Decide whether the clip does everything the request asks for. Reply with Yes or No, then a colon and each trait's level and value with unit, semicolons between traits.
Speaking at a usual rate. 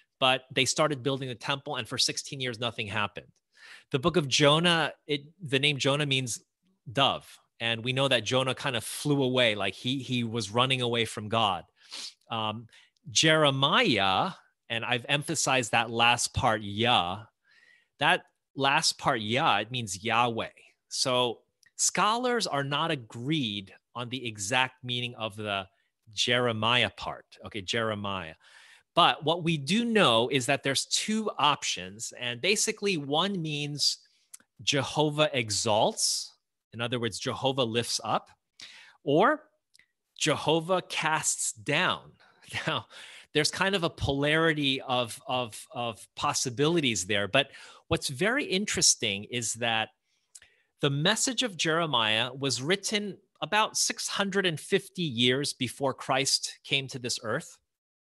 No: slow, 130 wpm